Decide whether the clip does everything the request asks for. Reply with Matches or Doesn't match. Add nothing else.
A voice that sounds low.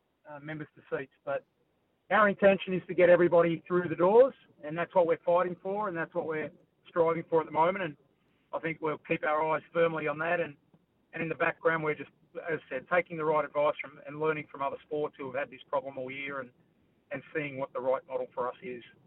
Doesn't match